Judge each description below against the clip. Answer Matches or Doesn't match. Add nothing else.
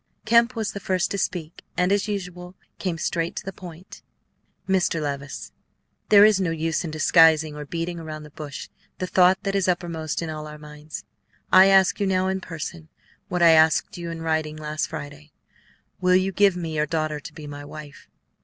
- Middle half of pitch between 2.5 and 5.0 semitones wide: Matches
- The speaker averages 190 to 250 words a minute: Matches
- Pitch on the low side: Doesn't match